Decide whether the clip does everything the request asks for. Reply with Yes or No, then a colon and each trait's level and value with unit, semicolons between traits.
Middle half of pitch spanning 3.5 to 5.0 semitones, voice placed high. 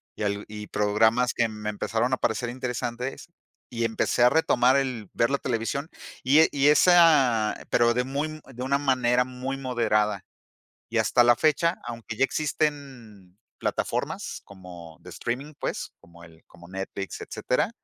No: average, 4.1 semitones; low, 120 Hz